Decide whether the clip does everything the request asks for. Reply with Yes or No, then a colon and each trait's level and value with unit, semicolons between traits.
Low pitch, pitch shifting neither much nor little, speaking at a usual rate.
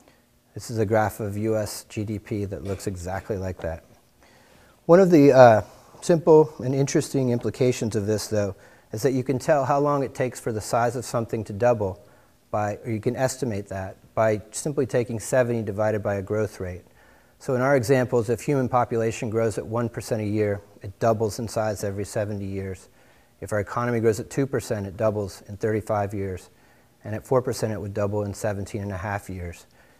Yes: low, 110 Hz; average, 3.2 semitones; average, 190 wpm